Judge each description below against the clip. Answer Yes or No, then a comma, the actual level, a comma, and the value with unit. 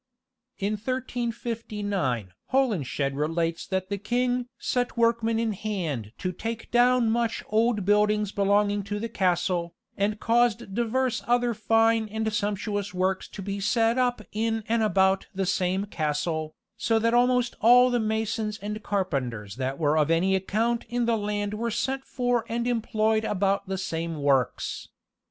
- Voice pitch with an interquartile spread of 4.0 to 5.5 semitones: No, average, 3.6 semitones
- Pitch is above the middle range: Yes, high, 210 Hz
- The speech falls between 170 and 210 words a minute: No, average, 150 wpm